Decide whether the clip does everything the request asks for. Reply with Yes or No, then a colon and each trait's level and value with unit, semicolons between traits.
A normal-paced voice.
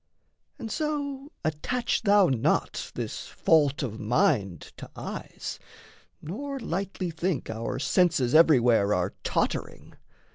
No: slow, 110 wpm